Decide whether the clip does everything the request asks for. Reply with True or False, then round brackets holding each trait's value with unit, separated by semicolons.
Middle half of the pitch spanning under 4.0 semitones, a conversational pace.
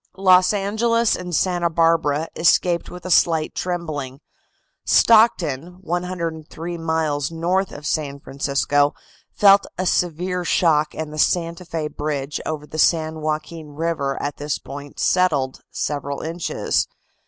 False (3.2 semitones; 130 wpm)